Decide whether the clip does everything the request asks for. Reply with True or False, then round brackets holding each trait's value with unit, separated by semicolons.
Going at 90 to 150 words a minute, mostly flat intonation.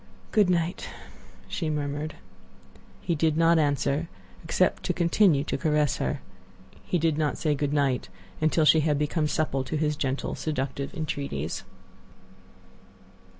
True (135 wpm; 2.3 semitones)